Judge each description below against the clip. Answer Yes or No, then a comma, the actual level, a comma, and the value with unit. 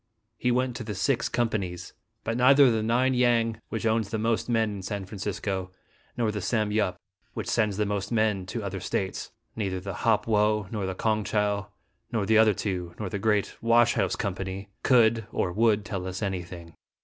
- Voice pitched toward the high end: No, low, 105 Hz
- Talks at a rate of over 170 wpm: Yes, average, 190 wpm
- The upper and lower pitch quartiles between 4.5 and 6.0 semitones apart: No, average, 2.8 semitones